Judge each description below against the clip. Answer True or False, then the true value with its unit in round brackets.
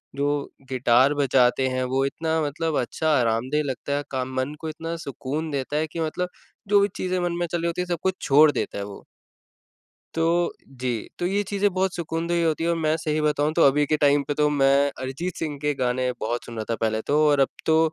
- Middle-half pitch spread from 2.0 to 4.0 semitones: True (3.7 semitones)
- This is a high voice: False (150 Hz)